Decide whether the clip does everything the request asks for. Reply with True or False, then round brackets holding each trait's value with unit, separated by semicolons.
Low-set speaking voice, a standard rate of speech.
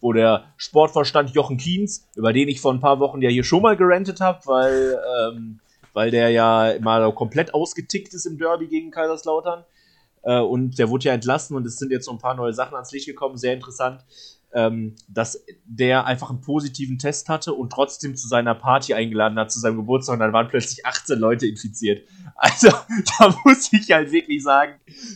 False (130 Hz; 200 wpm)